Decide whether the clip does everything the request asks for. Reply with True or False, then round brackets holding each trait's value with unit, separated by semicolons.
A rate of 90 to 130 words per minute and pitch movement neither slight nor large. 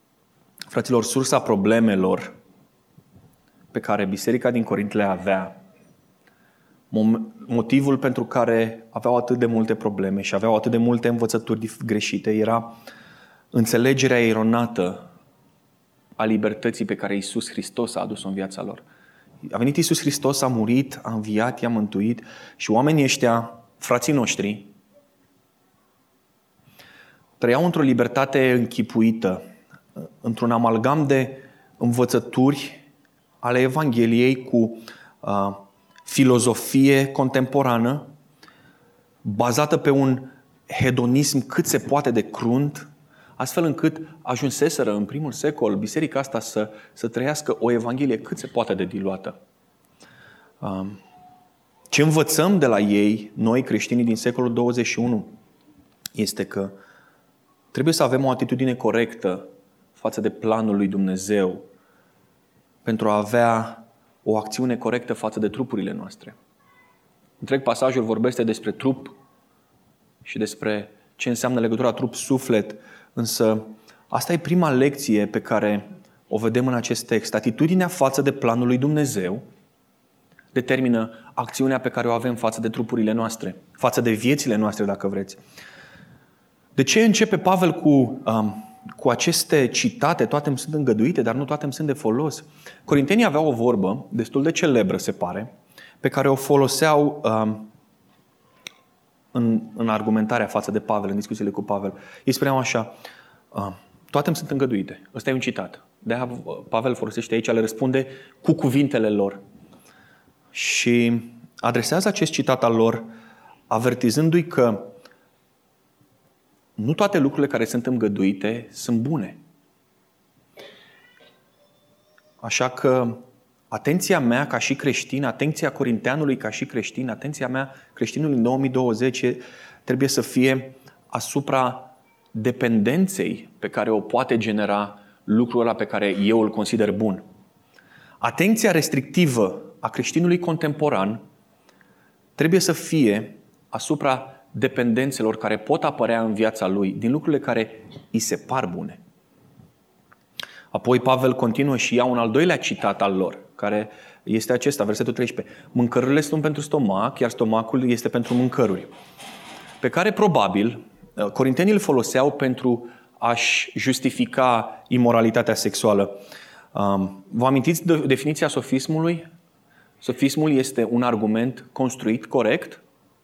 True (125 wpm; 3.7 semitones)